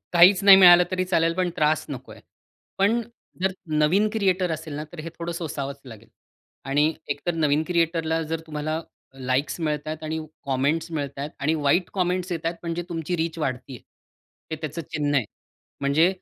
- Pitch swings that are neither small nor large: Yes, average, 3.1 semitones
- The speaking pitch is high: No, medium, 160 Hz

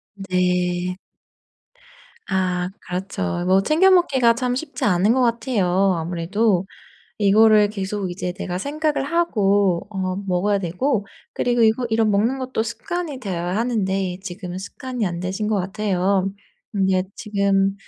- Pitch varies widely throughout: No, average, 4.1 semitones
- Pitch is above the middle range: Yes, high, 200 Hz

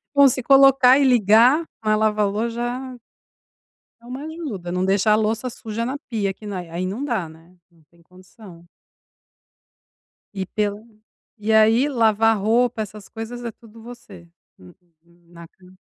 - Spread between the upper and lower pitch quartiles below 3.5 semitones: No, average, 4.0 semitones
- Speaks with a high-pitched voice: Yes, high, 220 Hz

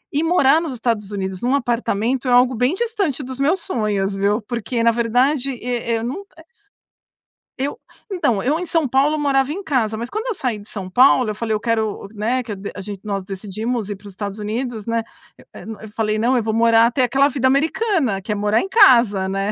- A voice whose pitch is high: Yes, high, 235 Hz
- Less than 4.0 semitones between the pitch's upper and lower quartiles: No, average, 4.4 semitones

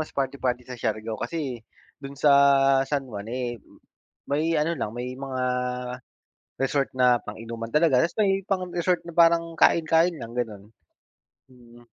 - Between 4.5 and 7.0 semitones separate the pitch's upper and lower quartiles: Yes, average, 5.3 semitones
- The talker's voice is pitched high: No, low, 130 Hz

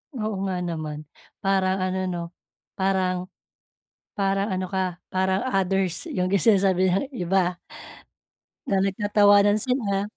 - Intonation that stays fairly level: Yes, narrow, 1.4 semitones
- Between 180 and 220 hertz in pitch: Yes, high, 190 Hz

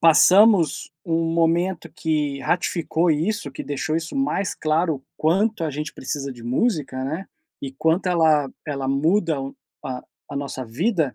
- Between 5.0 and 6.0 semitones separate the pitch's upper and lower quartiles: No, average, 3.7 semitones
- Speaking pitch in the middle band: Yes, medium, 160 Hz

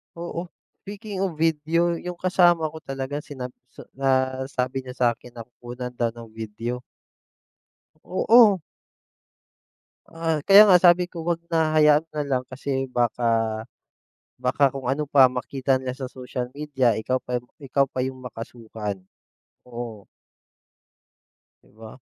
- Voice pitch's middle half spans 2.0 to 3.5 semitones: No, average, 4.6 semitones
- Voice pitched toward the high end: No, low, 130 Hz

